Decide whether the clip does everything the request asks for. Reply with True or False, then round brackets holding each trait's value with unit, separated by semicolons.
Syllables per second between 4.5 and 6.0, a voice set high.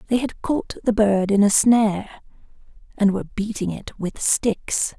False (4.3 syllables/s; 210 Hz)